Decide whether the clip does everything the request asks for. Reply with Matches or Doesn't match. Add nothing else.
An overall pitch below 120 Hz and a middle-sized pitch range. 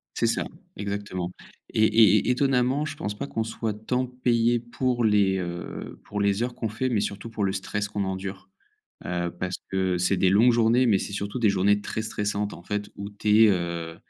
Matches